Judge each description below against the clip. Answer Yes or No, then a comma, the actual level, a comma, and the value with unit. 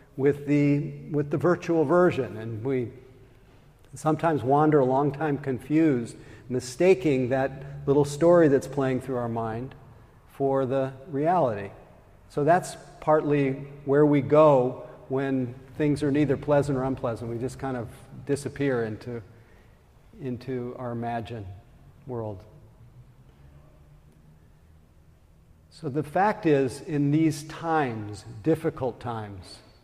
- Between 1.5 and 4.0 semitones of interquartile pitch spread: Yes, average, 3.7 semitones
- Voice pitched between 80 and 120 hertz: No, low, 130 Hz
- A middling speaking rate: No, slow, 115 wpm